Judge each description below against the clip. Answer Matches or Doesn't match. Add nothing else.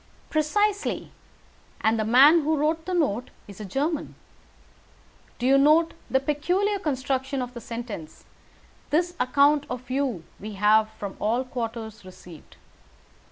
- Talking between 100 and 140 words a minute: Matches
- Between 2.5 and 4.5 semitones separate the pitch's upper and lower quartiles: Doesn't match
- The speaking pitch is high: Matches